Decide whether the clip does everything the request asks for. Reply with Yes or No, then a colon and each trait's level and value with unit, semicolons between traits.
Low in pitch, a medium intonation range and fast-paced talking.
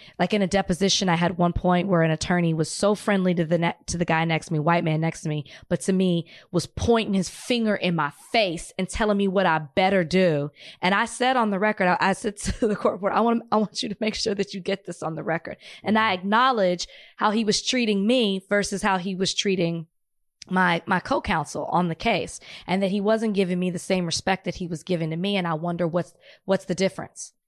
No: medium, 185 Hz; average, 3.1 semitones; fast, 250 wpm